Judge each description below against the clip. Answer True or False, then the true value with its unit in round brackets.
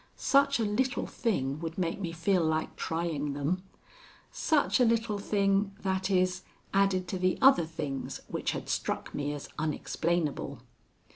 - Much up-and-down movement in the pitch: False (4.2 semitones)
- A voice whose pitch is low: False (185 Hz)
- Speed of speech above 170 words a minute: False (150 wpm)